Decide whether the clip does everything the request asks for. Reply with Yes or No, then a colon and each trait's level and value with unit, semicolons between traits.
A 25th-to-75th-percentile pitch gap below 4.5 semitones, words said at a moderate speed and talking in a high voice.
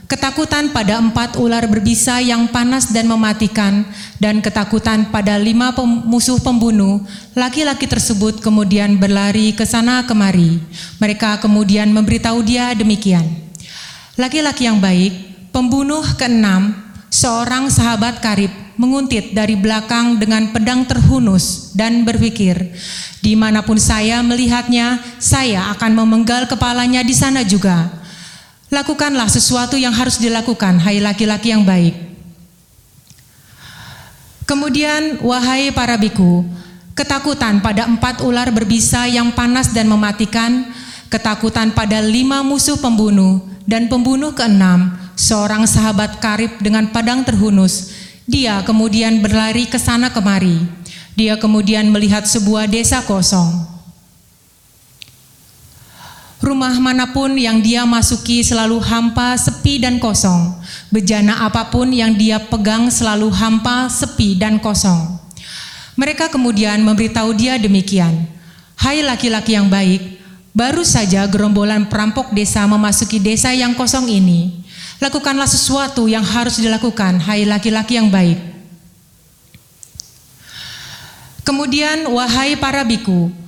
Yes: average, 3.3 semitones; average, 110 wpm; high, 220 Hz